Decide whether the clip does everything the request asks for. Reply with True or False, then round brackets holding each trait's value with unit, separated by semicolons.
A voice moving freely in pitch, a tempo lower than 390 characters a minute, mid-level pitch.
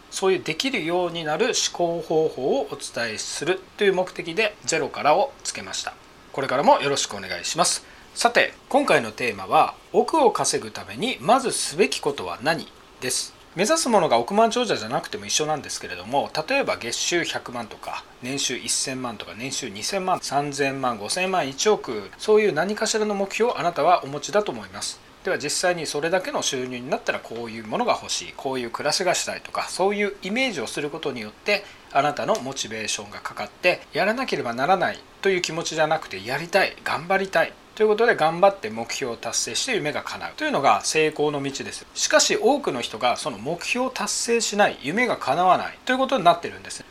True (6.4 semitones; 375 characters per minute; 180 Hz)